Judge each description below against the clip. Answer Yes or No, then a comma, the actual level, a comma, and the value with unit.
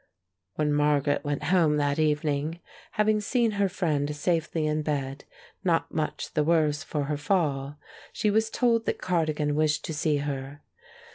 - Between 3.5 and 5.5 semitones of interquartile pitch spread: No, average, 2.8 semitones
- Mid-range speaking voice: Yes, medium, 150 Hz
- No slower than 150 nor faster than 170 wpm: Yes, average, 155 wpm